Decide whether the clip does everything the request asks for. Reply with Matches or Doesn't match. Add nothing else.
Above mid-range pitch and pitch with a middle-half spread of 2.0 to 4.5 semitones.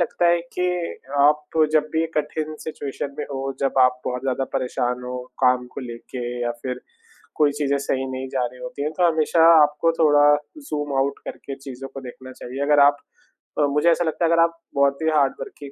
Doesn't match